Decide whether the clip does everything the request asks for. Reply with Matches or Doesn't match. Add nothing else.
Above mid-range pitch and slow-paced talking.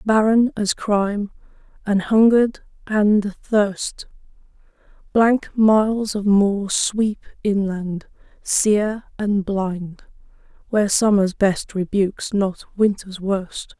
Matches